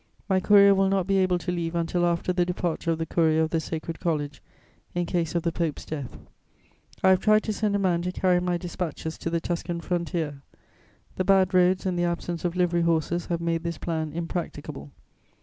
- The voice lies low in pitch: No, medium, 175 Hz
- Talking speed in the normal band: No, fast, 210 wpm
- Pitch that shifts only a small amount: Yes, narrow, 1.7 semitones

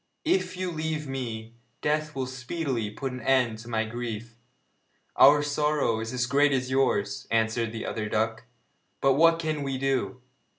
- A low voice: Yes, low, 130 Hz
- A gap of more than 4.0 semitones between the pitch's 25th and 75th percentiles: Yes, average, 4.5 semitones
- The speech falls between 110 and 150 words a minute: No, average, 165 wpm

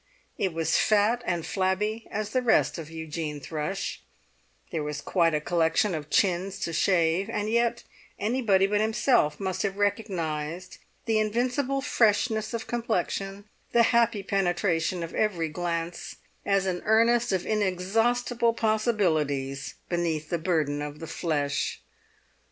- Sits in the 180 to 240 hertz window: Yes, high, 190 Hz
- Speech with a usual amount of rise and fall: Yes, average, 4.9 semitones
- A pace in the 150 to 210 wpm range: No, slow, 135 wpm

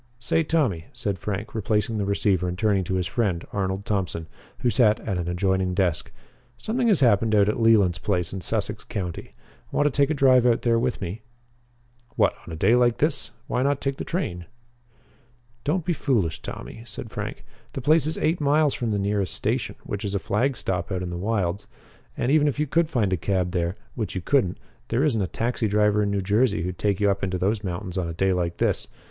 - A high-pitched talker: No, low, 105 Hz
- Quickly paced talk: Yes, fast, 215 wpm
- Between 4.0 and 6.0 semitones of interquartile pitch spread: Yes, average, 5.0 semitones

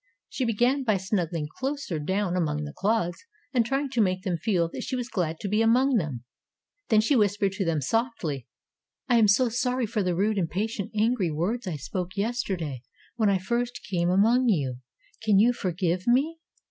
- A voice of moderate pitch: No, high, 205 Hz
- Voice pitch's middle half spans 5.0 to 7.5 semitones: Yes, average, 5.3 semitones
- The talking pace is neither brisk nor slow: Yes, average, 185 wpm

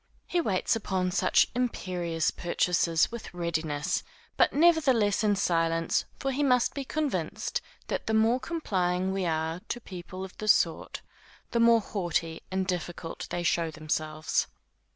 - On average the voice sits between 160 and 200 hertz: Yes, medium, 185 Hz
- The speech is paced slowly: No, average, 145 wpm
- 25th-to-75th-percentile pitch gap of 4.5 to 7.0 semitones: Yes, wide, 5.6 semitones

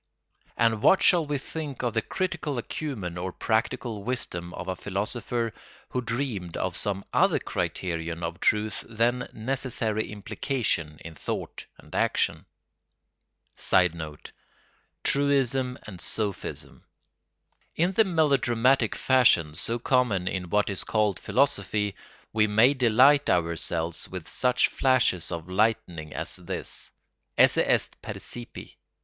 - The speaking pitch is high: No, low, 110 Hz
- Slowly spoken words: Yes, slow, 120 wpm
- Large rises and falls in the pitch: Yes, wide, 5.8 semitones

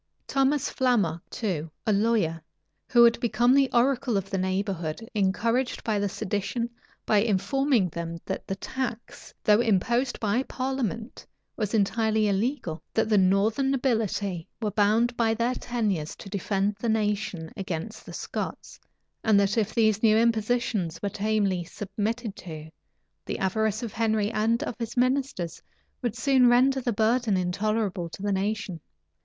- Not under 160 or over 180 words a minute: No, average, 150 wpm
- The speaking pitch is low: No, high, 215 Hz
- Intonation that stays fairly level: No, average, 3.3 semitones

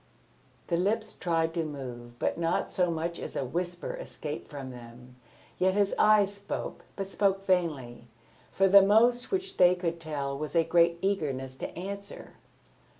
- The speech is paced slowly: No, average, 160 wpm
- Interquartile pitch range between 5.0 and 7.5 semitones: Yes, average, 5.3 semitones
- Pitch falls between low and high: Yes, medium, 170 Hz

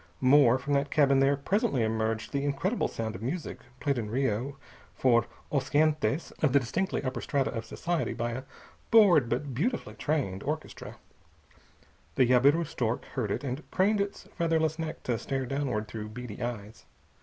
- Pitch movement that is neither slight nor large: Yes, average, 4.7 semitones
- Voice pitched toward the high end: No, low, 135 Hz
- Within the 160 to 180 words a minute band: Yes, average, 165 wpm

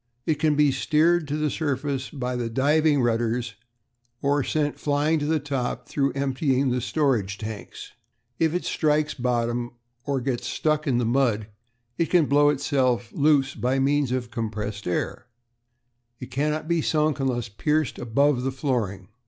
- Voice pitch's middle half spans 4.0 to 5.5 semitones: No, average, 3.6 semitones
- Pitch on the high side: No, low, 135 Hz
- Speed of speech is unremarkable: Yes, average, 160 wpm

